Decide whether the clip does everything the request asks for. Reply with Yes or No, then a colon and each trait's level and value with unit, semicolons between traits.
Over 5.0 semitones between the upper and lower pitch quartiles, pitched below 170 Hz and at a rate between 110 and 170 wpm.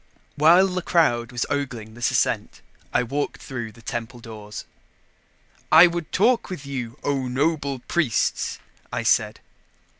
Yes: wide, 5.5 semitones; low, 135 Hz; average, 140 wpm